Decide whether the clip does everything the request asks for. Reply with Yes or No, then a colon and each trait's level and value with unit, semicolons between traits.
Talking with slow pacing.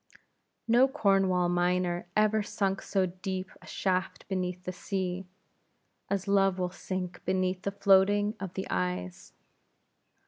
Yes: slow, 130 wpm